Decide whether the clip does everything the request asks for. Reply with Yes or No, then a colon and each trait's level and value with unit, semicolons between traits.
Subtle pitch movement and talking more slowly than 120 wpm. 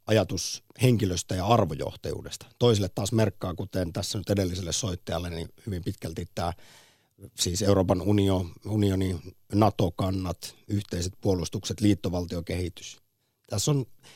No: average, 3.2 semitones; average, 110 wpm